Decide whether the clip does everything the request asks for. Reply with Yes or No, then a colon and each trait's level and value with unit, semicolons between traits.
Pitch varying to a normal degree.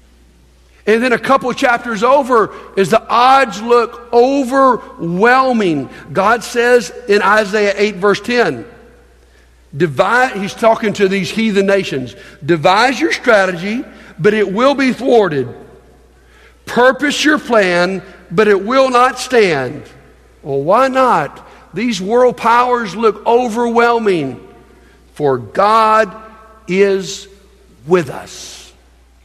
Yes: average, 4.7 semitones